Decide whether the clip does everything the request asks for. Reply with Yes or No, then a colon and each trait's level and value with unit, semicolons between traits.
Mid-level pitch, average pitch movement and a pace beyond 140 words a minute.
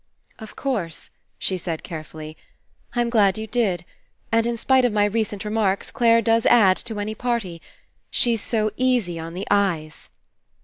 No: high, 210 Hz; average, 4.0 semitones; average, 165 wpm